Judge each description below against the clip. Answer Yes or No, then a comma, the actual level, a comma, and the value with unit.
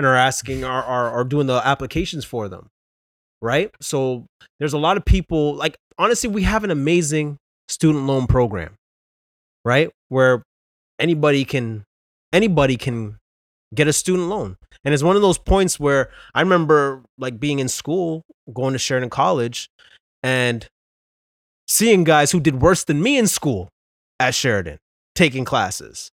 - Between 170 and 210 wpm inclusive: No, average, 155 wpm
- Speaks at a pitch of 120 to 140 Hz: Yes, low, 135 Hz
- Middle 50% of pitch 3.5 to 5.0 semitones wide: Yes, average, 4.6 semitones